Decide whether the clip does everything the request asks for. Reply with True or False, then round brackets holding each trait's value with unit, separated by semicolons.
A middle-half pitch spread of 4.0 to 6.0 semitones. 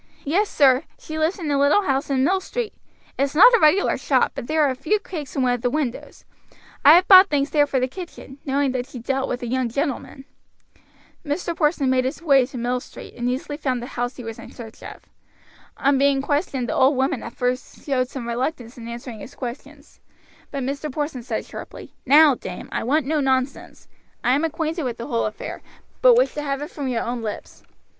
False (3.3 semitones)